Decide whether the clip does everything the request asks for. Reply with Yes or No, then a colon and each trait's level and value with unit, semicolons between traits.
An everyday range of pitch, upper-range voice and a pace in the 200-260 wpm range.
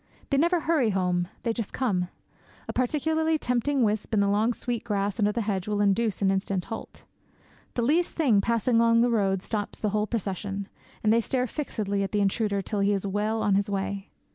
Yes: average, 3.2 semitones; high, 210 Hz; fast, 205 wpm